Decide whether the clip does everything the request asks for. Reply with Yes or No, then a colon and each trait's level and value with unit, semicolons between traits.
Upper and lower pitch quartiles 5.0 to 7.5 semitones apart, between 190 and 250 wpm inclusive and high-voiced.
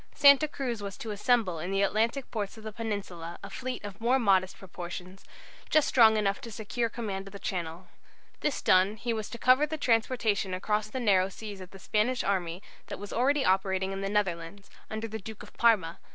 No: average, 3.5 semitones; fast, 205 wpm; high, 210 Hz